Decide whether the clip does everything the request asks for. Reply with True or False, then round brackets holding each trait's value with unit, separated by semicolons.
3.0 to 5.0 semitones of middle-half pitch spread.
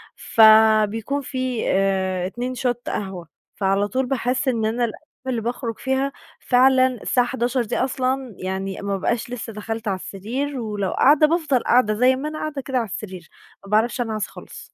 True (3.7 semitones)